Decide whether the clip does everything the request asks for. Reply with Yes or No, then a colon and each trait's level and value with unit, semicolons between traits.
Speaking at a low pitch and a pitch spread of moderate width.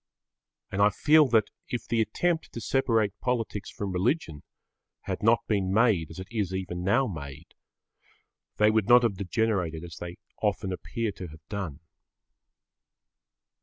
Yes: low, 100 Hz; average, 4.2 semitones